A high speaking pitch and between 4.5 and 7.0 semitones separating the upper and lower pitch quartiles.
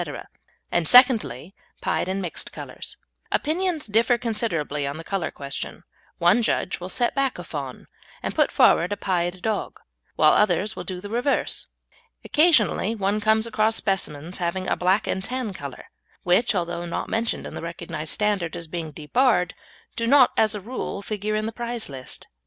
Yes: high, 200 Hz; average, 4.9 semitones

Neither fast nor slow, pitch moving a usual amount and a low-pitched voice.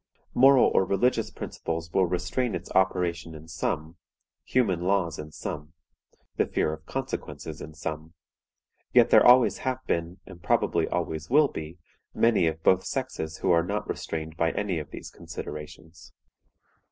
Yes: average, 155 wpm; average, 3.7 semitones; very low, 85 Hz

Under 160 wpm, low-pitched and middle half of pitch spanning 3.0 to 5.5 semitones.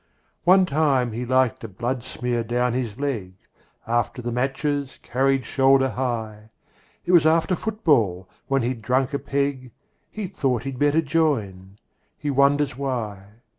Yes: average, 140 wpm; low, 130 Hz; average, 3.3 semitones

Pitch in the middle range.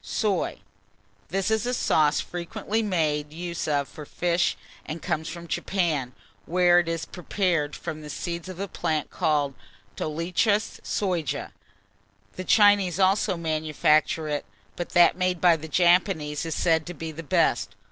Yes: medium, 170 Hz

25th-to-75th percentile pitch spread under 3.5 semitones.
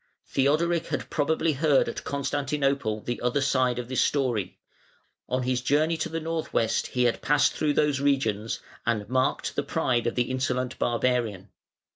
Yes: average, 3.1 semitones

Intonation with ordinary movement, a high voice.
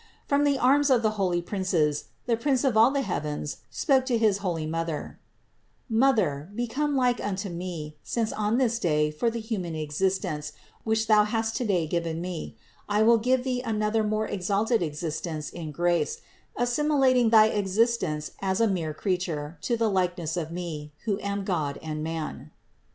No: wide, 5.9 semitones; high, 200 Hz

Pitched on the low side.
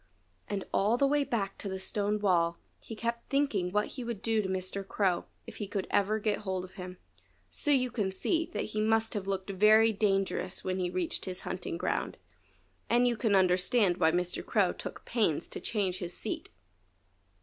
No: high, 200 Hz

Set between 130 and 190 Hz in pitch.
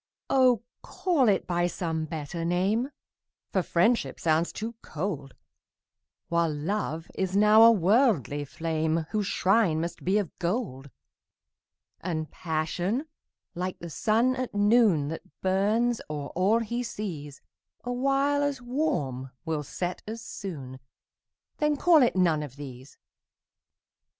Yes: medium, 185 Hz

